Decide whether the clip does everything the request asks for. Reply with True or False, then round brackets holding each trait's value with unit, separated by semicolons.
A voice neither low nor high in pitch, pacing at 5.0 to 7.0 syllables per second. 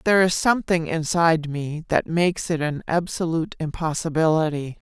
True (165 Hz; 5.5 syllables/s)